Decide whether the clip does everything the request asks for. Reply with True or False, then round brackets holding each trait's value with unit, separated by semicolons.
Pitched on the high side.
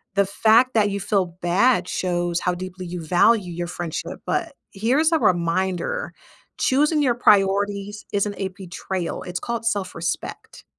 True (195 Hz)